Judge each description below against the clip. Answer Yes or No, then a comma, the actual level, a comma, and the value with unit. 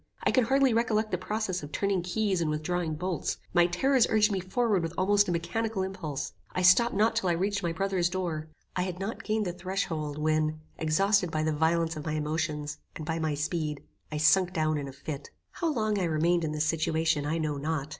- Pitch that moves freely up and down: No, average, 4.0 semitones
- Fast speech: Yes, fast, 215 wpm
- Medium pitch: Yes, medium, 175 Hz